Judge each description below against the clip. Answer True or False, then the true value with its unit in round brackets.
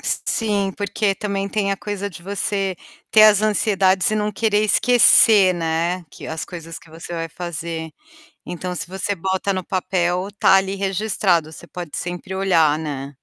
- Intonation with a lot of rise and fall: False (2.9 semitones)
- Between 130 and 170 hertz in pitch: False (190 Hz)